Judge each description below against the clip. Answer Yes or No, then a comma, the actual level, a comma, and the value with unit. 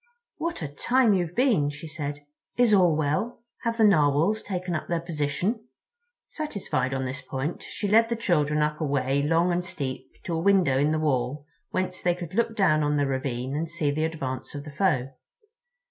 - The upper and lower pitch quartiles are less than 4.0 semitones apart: No, average, 5.0 semitones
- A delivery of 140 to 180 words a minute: No, average, 195 wpm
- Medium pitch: Yes, medium, 160 Hz